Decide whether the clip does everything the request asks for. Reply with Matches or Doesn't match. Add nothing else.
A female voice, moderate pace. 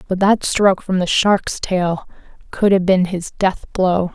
Matches